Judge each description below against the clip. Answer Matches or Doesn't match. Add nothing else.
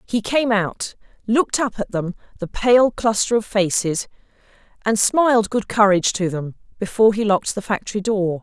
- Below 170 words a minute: Matches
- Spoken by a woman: Matches